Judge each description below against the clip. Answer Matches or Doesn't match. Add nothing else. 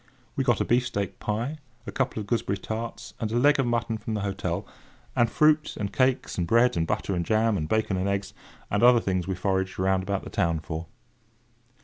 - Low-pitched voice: Matches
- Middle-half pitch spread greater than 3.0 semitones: Matches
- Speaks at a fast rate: Matches